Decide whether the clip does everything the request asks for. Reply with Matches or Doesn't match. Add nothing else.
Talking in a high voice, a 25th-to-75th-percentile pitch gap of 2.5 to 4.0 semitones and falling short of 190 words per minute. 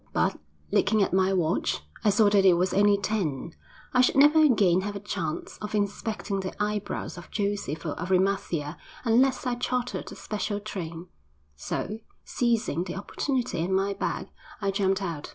Matches